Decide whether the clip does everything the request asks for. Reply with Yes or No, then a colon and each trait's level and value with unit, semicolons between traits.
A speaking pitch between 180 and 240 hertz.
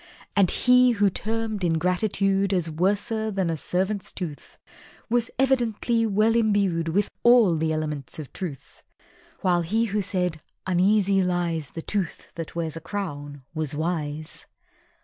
Yes: medium, 185 Hz